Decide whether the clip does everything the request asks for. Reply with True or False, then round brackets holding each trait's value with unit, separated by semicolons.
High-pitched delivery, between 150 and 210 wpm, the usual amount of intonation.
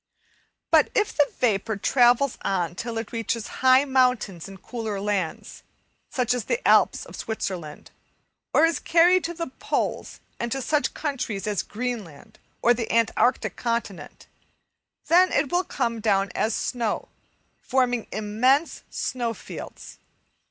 False (235 Hz; 140 wpm; 4.1 semitones)